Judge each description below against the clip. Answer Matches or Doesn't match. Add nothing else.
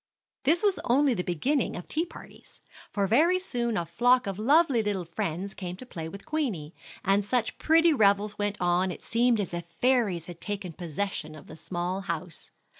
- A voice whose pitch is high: Matches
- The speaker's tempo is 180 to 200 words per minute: Matches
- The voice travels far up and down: Matches